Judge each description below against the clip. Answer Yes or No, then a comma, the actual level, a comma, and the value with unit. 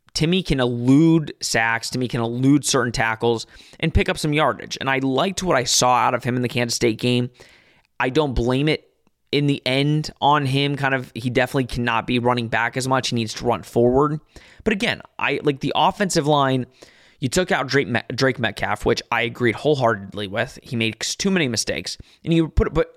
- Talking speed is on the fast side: Yes, fast, 210 wpm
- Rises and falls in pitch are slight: No, average, 3.7 semitones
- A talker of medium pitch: No, low, 130 Hz